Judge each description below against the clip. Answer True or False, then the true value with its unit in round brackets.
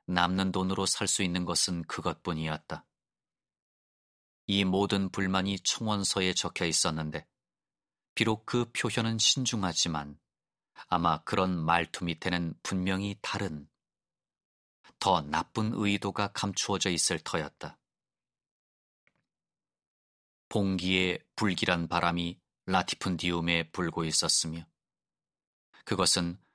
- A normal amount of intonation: True (3.0 semitones)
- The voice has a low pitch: True (90 Hz)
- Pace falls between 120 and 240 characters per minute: True (220 characters per minute)